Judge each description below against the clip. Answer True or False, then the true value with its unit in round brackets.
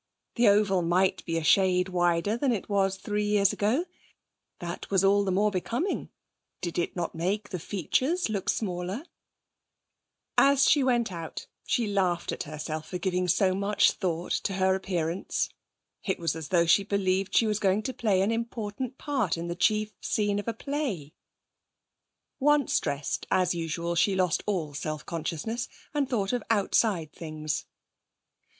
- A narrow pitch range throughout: False (3.7 semitones)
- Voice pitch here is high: True (195 Hz)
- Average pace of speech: True (165 wpm)